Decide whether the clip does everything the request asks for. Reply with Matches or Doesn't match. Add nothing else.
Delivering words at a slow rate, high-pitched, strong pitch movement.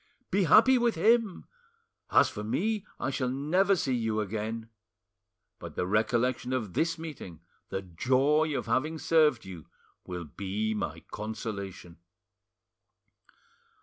Doesn't match